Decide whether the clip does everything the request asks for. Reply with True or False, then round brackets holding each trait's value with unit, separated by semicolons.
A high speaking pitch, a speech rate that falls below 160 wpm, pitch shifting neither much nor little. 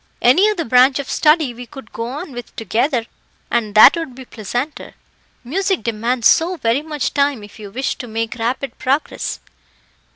False (255 Hz; 170 wpm; 4.4 semitones)